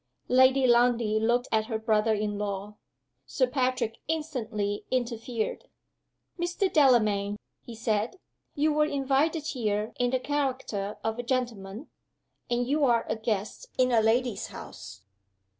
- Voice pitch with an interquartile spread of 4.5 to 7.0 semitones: No, average, 3.3 semitones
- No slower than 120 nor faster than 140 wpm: Yes, slow, 135 wpm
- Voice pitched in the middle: No, high, 240 Hz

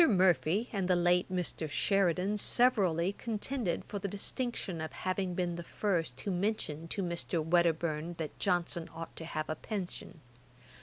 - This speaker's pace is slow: No, average, 155 wpm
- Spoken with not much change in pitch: No, average, 3.1 semitones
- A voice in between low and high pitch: Yes, medium, 180 Hz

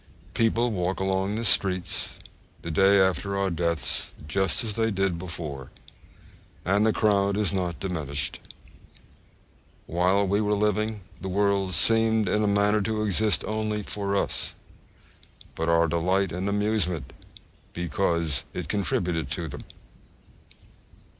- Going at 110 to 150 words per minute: Yes, slow, 135 wpm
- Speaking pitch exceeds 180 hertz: No, very low, 95 Hz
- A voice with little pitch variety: No, average, 3.2 semitones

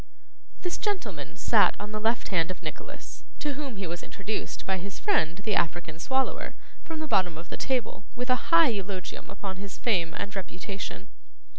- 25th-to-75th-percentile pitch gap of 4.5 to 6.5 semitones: Yes, wide, 5.5 semitones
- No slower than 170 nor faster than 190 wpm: Yes, average, 180 wpm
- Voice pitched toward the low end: No, high, 200 Hz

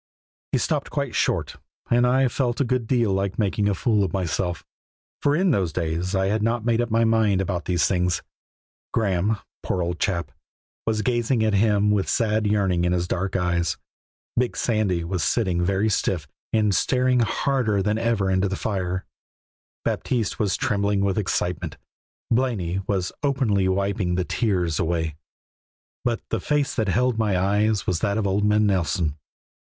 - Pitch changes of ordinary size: Yes, average, 3.6 semitones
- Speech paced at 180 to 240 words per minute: No, average, 170 wpm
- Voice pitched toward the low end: Yes, low, 100 Hz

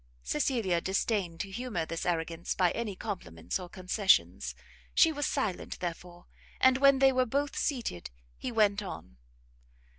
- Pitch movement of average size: No, wide, 6.6 semitones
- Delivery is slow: No, average, 145 wpm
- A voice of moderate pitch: No, high, 195 Hz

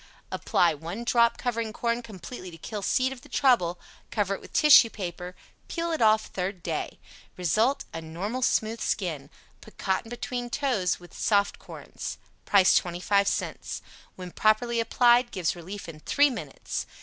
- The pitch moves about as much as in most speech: Yes, average, 5.0 semitones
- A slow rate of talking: No, average, 160 wpm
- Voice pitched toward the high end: Yes, high, 215 Hz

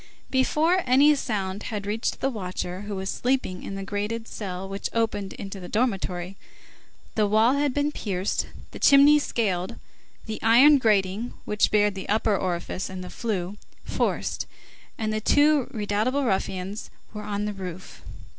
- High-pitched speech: Yes, high, 210 Hz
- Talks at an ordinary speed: Yes, average, 155 wpm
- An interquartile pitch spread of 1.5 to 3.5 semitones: No, average, 4.1 semitones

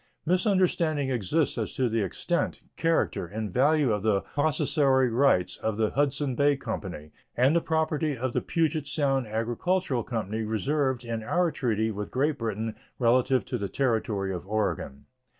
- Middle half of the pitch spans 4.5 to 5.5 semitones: Yes, average, 5.1 semitones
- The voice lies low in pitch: Yes, low, 125 Hz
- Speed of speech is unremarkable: Yes, average, 155 wpm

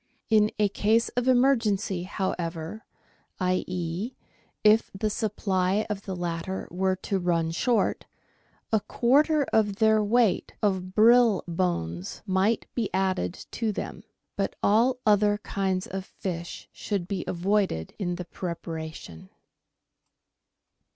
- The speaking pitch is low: No, high, 195 Hz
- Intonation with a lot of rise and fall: No, average, 3.4 semitones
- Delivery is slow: Yes, slow, 120 wpm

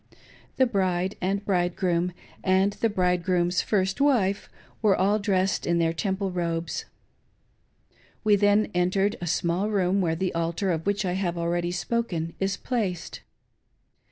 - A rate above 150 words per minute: No, average, 140 wpm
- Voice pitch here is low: No, medium, 185 Hz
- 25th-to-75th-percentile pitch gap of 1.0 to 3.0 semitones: Yes, narrow, 2.5 semitones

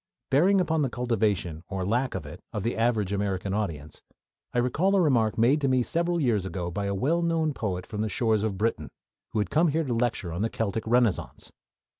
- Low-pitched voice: Yes, low, 115 Hz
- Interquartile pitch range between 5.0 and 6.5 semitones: Yes, wide, 5.5 semitones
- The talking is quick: Yes, fast, 215 wpm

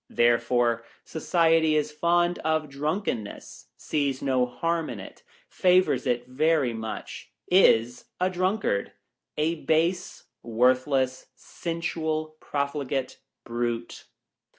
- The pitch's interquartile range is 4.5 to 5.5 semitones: Yes, average, 5.1 semitones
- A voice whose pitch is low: No, medium, 150 Hz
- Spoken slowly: Yes, slow, 110 wpm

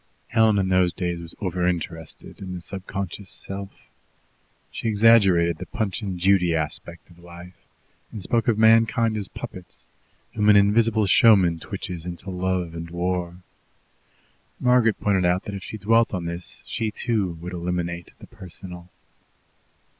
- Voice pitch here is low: Yes, very low, 95 Hz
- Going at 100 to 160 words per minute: Yes, average, 150 wpm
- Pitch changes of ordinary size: Yes, average, 3.3 semitones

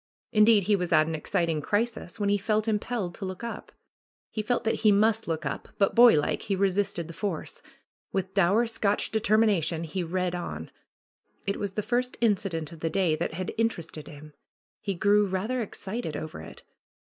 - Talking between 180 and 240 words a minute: Yes, average, 190 wpm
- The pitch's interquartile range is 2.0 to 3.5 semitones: No, average, 4.2 semitones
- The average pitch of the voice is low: No, high, 195 Hz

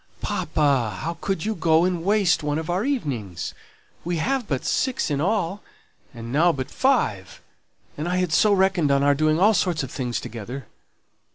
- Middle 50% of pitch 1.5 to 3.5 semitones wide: No, wide, 5.6 semitones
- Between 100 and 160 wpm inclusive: No, average, 180 wpm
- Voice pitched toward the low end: No, medium, 160 Hz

